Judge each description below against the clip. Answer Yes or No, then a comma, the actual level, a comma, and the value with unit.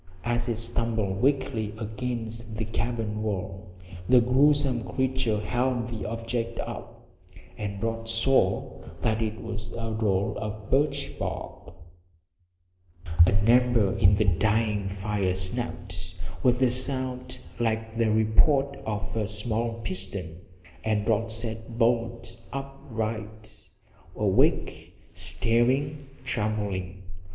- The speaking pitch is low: Yes, low, 115 Hz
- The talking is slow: Yes, slow, 110 wpm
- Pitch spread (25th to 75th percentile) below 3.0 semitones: Yes, narrow, 2.4 semitones